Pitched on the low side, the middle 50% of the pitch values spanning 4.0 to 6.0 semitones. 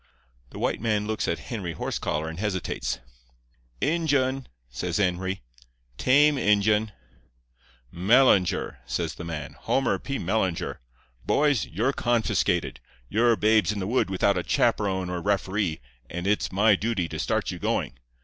Yes: low, 100 Hz; average, 4.6 semitones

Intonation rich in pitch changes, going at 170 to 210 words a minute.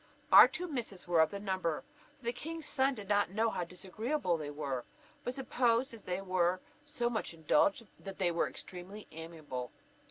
Yes: wide, 5.8 semitones; average, 185 wpm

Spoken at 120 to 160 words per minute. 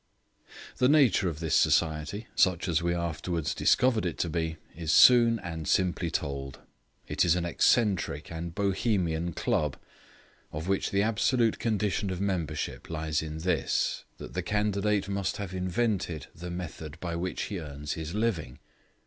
Yes: average, 155 wpm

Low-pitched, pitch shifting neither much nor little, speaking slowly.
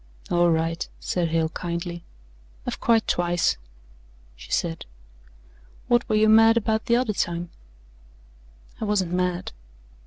No: medium, 175 Hz; average, 4.3 semitones; slow, 125 wpm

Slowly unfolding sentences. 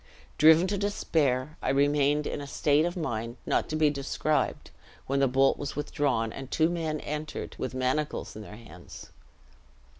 No: average, 170 wpm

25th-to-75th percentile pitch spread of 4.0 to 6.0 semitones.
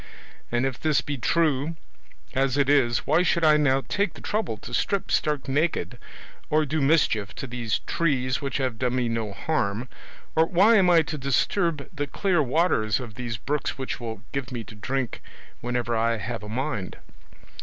Yes: average, 4.7 semitones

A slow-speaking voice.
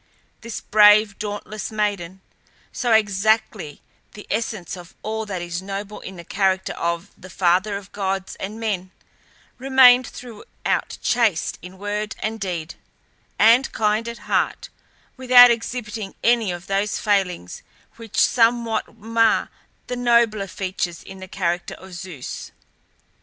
Yes: slow, 130 wpm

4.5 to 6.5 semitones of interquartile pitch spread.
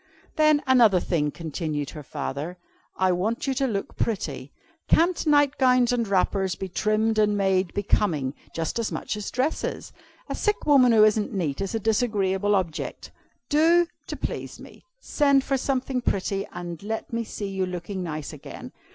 Yes: wide, 5.6 semitones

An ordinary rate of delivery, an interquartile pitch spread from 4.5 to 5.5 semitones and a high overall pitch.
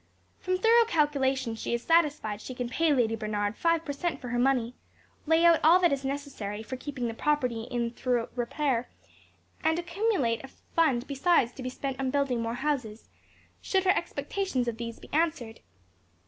Yes: average, 180 wpm; average, 5.2 semitones; very high, 265 Hz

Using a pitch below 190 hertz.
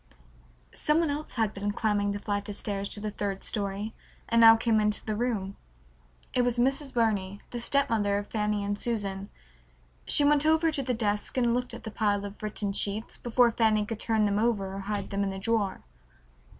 No: high, 215 Hz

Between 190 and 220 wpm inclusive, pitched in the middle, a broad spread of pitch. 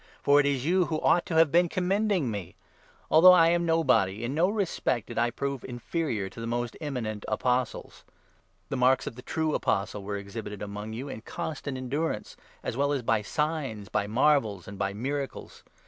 No: average, 195 wpm; low, 130 Hz; wide, 6.4 semitones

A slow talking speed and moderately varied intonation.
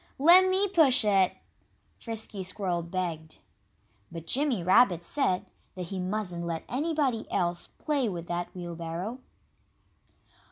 No: slow, 120 wpm; wide, 6.9 semitones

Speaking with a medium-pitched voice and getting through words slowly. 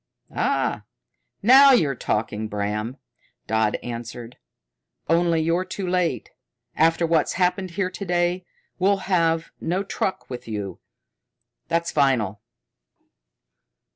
Yes: medium, 165 Hz; slow, 105 wpm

